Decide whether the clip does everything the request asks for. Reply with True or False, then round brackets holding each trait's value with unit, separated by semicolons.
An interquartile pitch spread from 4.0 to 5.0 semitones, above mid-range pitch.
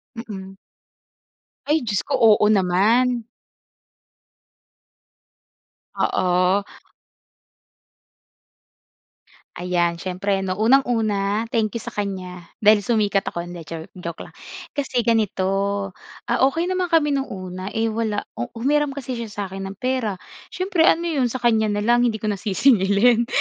True (4.3 semitones; 215 Hz)